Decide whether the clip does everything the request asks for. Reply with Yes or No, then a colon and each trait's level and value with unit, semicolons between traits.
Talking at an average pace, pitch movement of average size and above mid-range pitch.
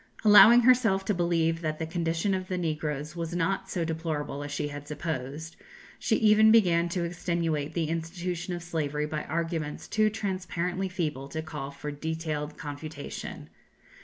No: average, 160 wpm; average, 3.0 semitones; medium, 165 Hz